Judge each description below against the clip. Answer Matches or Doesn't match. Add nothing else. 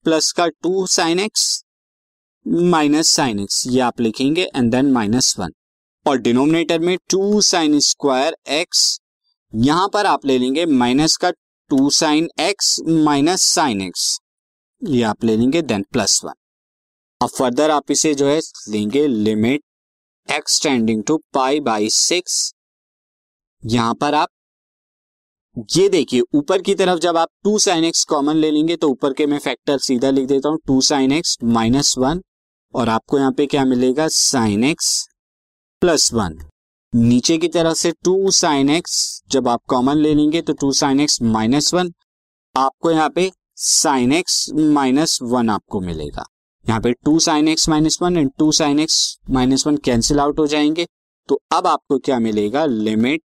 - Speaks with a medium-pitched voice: Matches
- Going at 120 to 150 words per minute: Doesn't match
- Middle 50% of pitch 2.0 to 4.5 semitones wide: Doesn't match